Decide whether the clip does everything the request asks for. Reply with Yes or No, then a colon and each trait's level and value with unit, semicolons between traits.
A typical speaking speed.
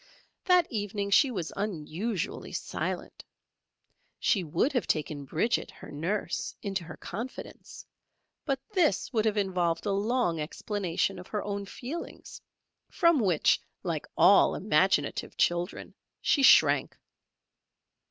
No: slow, 120 wpm